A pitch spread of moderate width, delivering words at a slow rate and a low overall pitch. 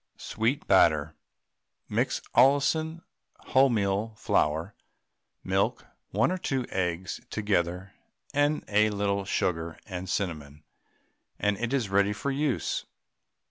No: wide, 6.3 semitones; slow, 105 wpm; low, 105 Hz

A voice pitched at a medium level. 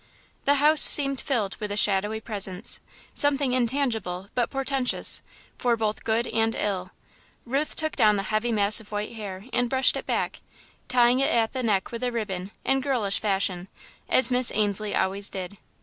No: high, 225 Hz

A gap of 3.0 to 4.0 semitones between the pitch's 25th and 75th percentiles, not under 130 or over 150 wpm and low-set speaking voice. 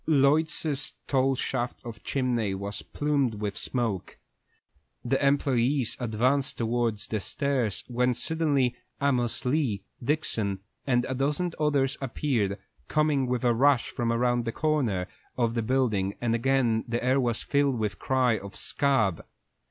Yes: average, 3.4 semitones; average, 145 wpm; low, 125 Hz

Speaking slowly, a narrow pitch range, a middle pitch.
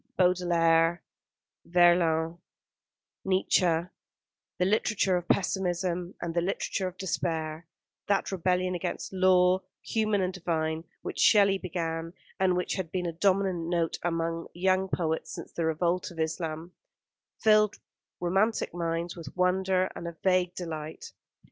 Yes: slow, 130 wpm; narrow, 2.1 semitones; medium, 175 Hz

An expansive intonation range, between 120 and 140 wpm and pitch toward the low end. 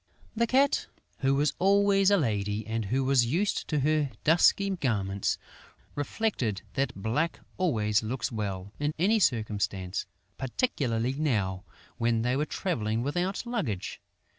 Yes: wide, 8.4 semitones; slow, 135 wpm; low, 130 Hz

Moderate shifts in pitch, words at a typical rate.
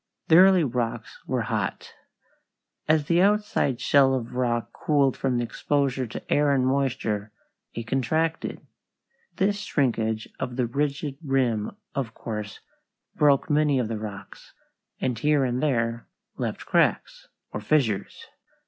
No: average, 4.0 semitones; slow, 130 wpm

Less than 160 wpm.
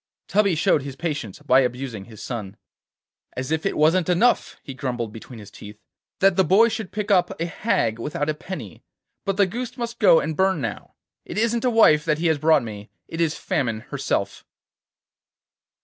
No: average, 185 wpm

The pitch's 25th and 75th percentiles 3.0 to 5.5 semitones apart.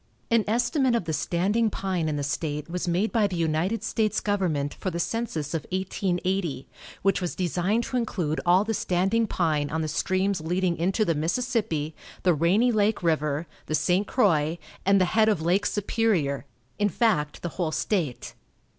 Yes: average, 4.7 semitones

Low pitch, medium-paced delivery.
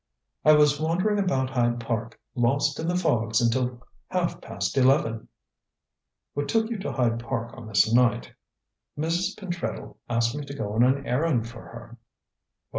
Yes: low, 130 Hz; average, 160 wpm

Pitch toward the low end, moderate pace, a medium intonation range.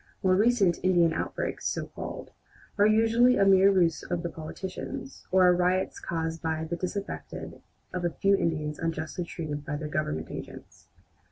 No: medium, 175 Hz; average, 165 wpm; average, 3.1 semitones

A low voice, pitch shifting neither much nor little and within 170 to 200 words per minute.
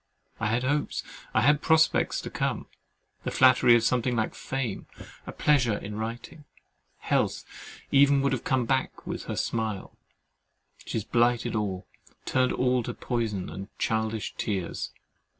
No: low, 120 Hz; average, 3.1 semitones; average, 145 wpm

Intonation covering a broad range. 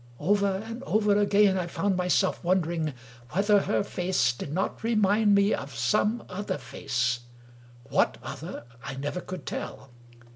Yes: wide, 6.3 semitones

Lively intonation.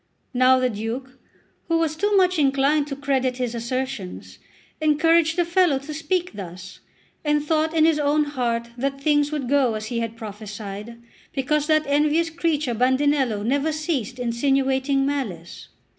No: average, 4.2 semitones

